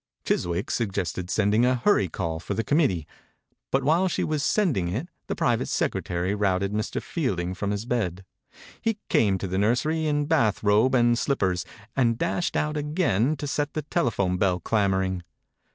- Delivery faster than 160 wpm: Yes, average, 170 wpm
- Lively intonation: Yes, wide, 7.6 semitones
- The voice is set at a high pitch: No, low, 110 Hz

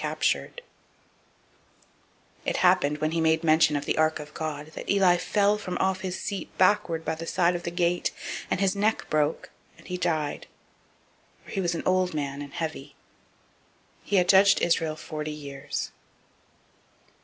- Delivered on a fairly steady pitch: No, average, 3.3 semitones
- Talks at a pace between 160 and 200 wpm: Yes, average, 165 wpm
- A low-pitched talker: No, medium, 165 Hz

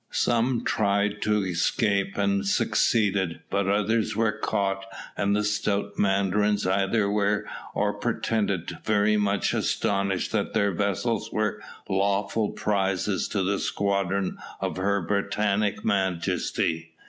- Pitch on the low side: Yes, low, 100 Hz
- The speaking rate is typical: No, slow, 125 wpm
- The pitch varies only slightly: Yes, narrow, 1.3 semitones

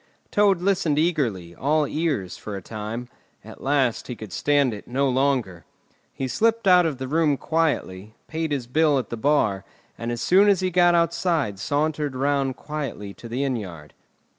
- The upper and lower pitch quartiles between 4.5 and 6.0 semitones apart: Yes, wide, 5.6 semitones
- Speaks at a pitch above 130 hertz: Yes, medium, 140 Hz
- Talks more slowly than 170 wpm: No, average, 180 wpm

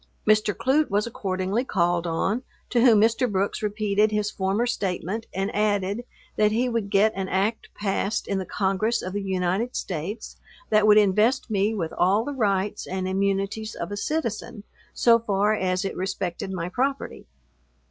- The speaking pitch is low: No, high, 205 Hz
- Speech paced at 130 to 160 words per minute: No, average, 170 wpm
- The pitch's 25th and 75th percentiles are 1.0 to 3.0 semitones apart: Yes, narrow, 2.5 semitones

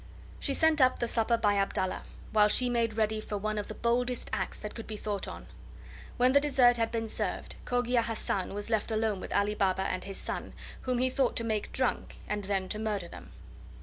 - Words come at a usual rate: No, fast, 215 wpm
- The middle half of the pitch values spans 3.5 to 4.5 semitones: No, average, 2.9 semitones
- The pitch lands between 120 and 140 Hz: No, high, 220 Hz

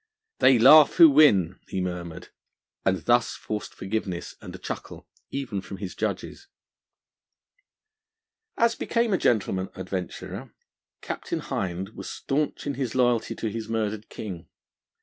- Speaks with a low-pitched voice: Yes, low, 110 Hz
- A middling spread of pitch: No, wide, 5.8 semitones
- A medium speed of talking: No, slow, 130 wpm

